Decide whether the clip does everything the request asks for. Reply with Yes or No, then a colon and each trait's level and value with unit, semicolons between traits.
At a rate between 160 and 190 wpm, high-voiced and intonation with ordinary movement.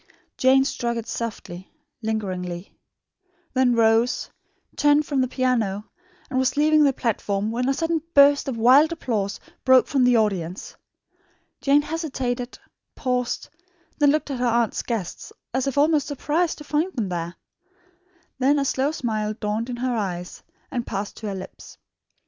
No: average, 150 wpm; very high, 250 Hz; average, 4.7 semitones